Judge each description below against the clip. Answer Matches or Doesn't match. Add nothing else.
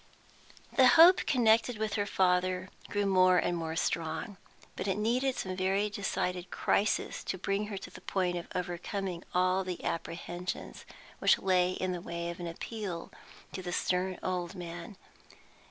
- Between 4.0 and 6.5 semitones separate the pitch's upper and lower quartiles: Doesn't match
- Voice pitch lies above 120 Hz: Matches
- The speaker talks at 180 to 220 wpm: Doesn't match